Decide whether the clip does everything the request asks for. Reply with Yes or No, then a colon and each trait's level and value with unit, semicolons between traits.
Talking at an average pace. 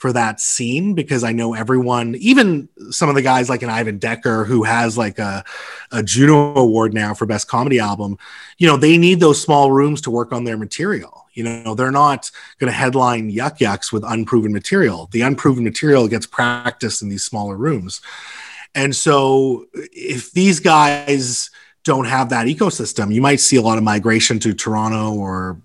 Yes: average, 185 wpm